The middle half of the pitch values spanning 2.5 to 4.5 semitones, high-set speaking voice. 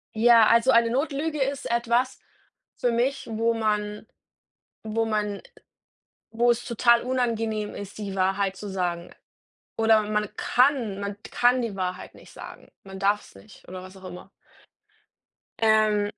Yes: average, 2.8 semitones; high, 220 Hz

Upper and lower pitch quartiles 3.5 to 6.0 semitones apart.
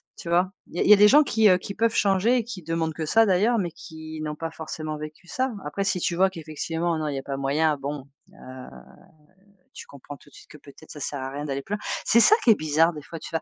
Yes: average, 4.7 semitones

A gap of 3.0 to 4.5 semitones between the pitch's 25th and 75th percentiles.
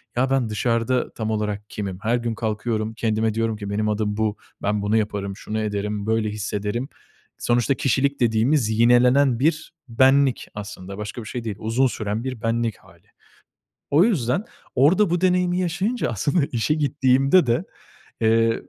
Yes: average, 3.9 semitones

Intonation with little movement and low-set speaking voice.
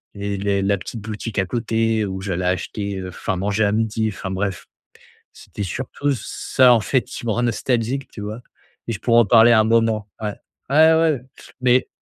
No: average, 3.0 semitones; low, 110 Hz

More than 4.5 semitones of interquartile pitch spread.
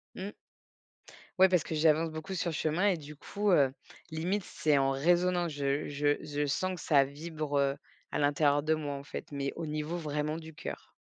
No: average, 2.8 semitones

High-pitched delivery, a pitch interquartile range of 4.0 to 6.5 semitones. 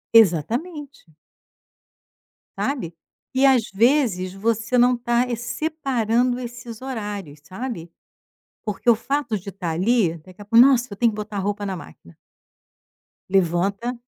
Yes: high, 225 Hz; average, 4.3 semitones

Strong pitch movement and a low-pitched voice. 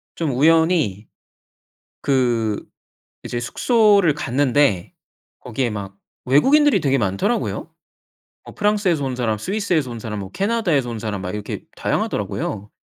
Yes: wide, 8.4 semitones; low, 130 Hz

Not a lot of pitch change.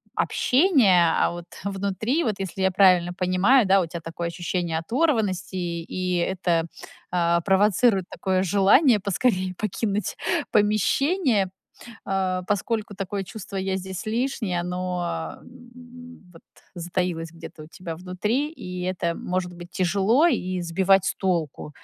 No: average, 3.3 semitones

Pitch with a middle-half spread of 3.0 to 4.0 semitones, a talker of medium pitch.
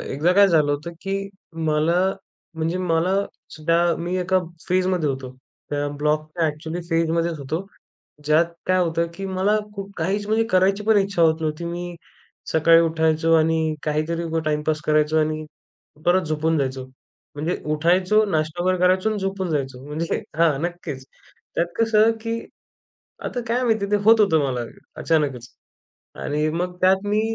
Yes: average, 3.4 semitones; medium, 165 Hz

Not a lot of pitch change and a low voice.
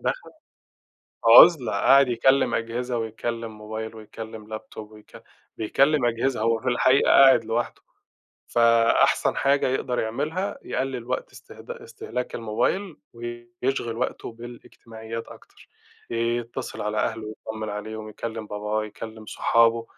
Yes: narrow, 2.1 semitones; low, 115 Hz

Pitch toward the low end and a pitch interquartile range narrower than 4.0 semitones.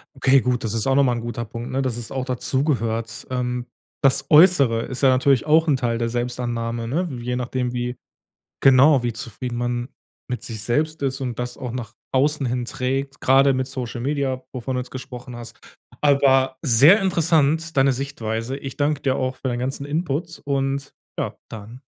Yes: low, 130 Hz; narrow, 2.4 semitones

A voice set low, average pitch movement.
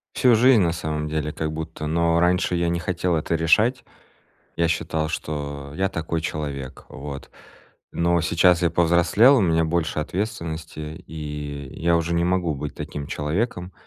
No: very low, 85 Hz; narrow, 2.3 semitones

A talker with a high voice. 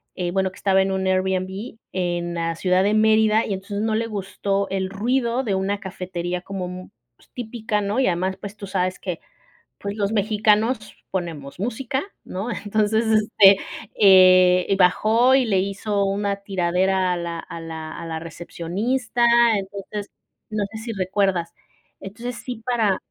Yes: high, 195 Hz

